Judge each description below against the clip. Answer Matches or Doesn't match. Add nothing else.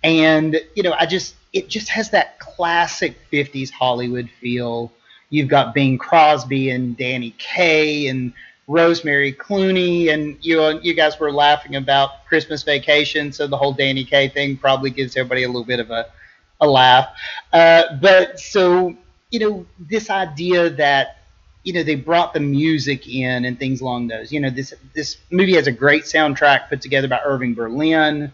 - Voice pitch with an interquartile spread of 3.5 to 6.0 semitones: Matches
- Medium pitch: Matches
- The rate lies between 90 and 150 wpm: Doesn't match